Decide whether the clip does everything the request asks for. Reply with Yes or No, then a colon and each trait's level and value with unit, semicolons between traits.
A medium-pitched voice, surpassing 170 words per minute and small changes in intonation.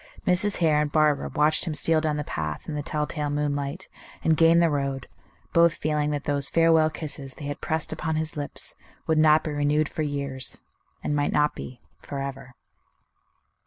Yes: medium, 150 Hz; average, 180 wpm; narrow, 1.6 semitones